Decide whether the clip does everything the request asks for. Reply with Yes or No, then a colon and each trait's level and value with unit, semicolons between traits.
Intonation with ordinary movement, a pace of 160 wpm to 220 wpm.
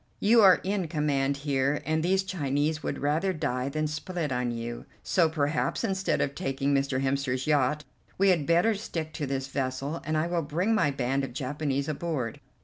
Yes: average, 3.6 semitones; average, 185 wpm